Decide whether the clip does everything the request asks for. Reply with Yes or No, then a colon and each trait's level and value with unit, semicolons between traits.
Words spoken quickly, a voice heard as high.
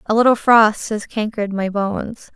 No: average, 180 wpm; high, 215 Hz